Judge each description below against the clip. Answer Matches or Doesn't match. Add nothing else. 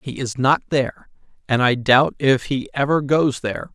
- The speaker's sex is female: Doesn't match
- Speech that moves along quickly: Doesn't match